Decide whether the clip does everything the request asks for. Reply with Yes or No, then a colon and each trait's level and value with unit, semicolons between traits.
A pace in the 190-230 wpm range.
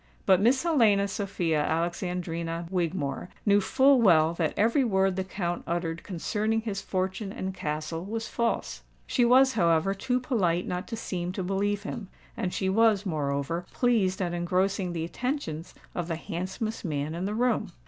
No: average, 165 wpm